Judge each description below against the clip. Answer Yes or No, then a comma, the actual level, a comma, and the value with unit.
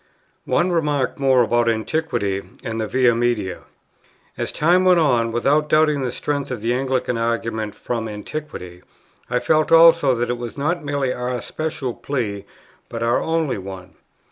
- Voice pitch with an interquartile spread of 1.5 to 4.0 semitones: No, average, 4.6 semitones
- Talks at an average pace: Yes, average, 160 wpm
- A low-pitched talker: Yes, low, 125 Hz